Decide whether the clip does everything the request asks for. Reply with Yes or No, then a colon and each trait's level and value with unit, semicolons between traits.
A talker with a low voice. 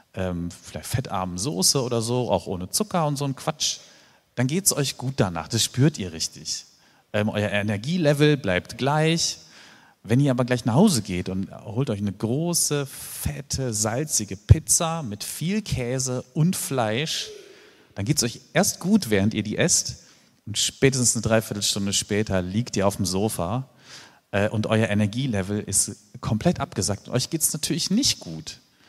Yes: low, 120 Hz